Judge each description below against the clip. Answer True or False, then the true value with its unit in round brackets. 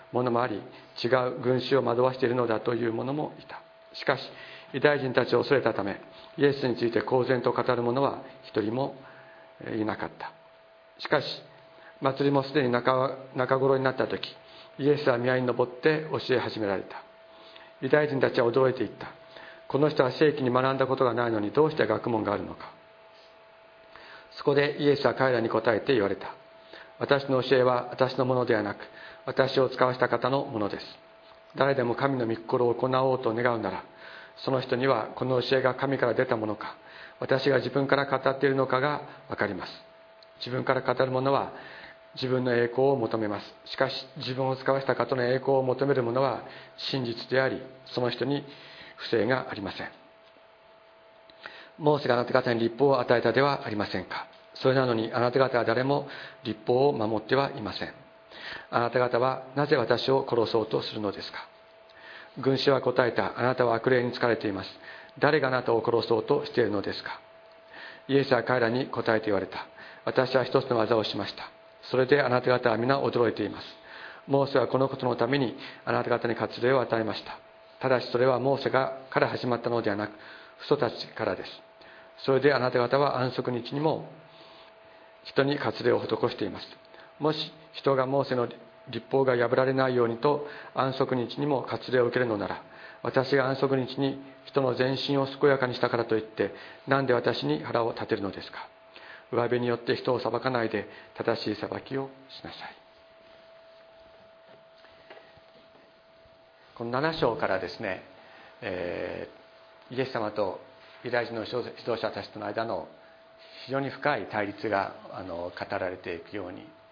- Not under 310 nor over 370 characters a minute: True (340 characters per minute)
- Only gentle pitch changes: True (2.2 semitones)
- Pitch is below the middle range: True (130 Hz)